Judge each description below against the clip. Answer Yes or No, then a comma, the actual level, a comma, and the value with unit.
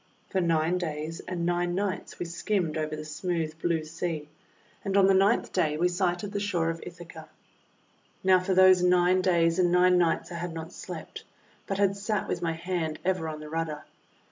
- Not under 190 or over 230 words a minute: Yes, average, 195 wpm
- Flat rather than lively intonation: Yes, narrow, 2.3 semitones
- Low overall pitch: No, medium, 175 Hz